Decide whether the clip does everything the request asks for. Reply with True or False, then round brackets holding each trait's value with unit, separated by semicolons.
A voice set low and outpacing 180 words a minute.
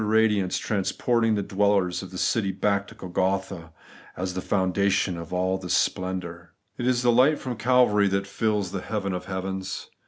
False (95 Hz; 165 wpm)